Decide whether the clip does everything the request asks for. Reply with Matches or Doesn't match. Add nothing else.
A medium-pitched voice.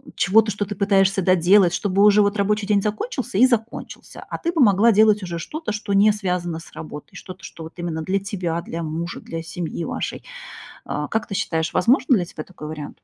Doesn't match